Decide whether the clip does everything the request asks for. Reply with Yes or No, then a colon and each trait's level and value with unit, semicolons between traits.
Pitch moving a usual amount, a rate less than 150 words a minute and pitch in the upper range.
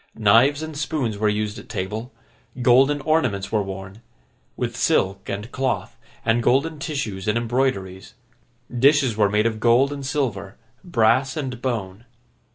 No: average, 4.5 semitones; average, 140 wpm; low, 115 Hz